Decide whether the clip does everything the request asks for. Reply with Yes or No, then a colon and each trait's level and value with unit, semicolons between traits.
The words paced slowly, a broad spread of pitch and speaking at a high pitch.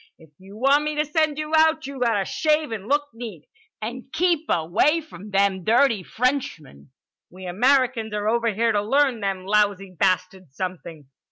No: average, 170 wpm; wide, 6.9 semitones; high, 225 Hz